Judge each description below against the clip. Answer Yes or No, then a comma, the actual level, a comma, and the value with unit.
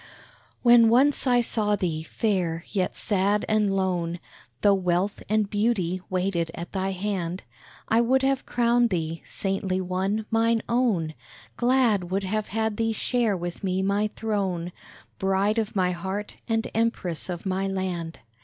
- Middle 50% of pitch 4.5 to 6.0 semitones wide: No, average, 3.4 semitones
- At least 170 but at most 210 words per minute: No, average, 150 wpm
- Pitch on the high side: Yes, high, 195 Hz